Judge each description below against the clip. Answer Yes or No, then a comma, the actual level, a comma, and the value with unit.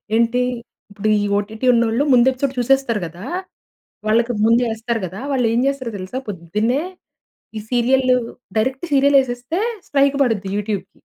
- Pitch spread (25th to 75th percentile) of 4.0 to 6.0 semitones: No, average, 3.3 semitones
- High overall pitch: Yes, high, 235 Hz